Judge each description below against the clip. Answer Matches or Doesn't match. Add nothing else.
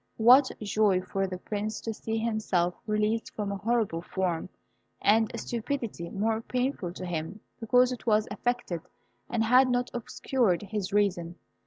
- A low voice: Doesn't match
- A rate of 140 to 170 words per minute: Matches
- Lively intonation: Doesn't match